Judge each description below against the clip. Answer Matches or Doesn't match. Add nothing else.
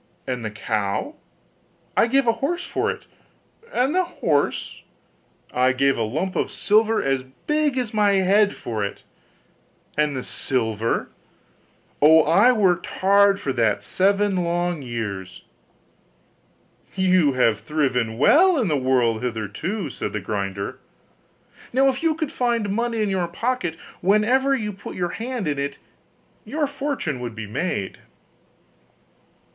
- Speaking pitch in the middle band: Matches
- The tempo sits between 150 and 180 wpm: Doesn't match